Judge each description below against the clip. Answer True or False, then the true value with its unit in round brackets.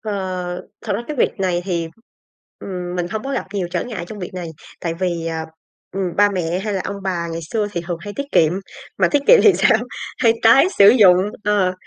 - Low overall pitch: False (190 Hz)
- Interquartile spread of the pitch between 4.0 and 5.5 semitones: False (3.3 semitones)